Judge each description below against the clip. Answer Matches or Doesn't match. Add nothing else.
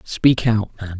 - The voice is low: Matches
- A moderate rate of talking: Matches